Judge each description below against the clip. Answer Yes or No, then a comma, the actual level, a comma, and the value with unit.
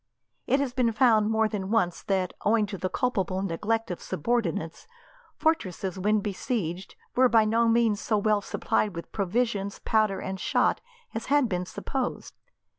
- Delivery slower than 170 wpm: Yes, average, 160 wpm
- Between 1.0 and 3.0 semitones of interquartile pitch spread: No, average, 3.4 semitones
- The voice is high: Yes, high, 215 Hz